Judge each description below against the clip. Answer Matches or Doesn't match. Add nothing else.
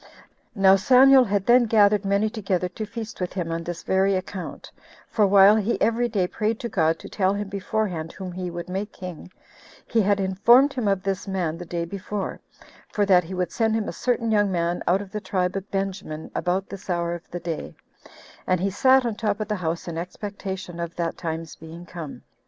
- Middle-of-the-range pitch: Doesn't match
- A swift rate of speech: Matches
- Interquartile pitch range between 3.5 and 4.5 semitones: Doesn't match